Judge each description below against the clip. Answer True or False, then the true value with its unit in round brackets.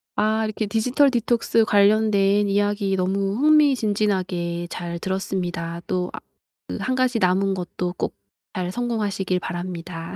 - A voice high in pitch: True (195 Hz)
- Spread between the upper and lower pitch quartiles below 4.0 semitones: True (3.2 semitones)